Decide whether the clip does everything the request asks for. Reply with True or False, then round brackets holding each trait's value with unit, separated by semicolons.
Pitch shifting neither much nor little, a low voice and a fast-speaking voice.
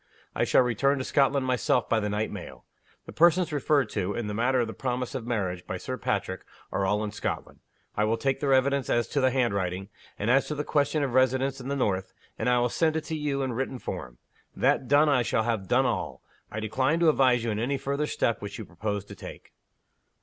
True (4.4 semitones; 125 Hz; 235 wpm)